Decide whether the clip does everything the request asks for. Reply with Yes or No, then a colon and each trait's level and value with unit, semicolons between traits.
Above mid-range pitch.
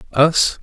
No: medium, 145 Hz